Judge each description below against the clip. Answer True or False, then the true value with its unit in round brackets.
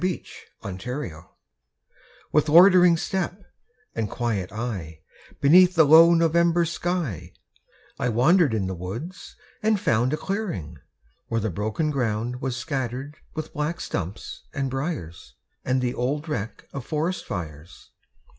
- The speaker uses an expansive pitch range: True (7.6 semitones)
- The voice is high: False (135 Hz)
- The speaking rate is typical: False (130 wpm)